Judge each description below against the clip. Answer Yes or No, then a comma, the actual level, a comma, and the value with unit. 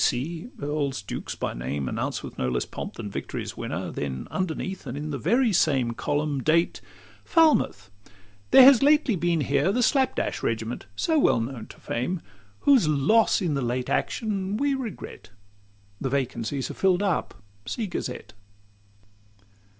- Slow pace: No, average, 160 wpm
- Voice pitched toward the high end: No, medium, 155 Hz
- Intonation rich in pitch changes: Yes, wide, 8.9 semitones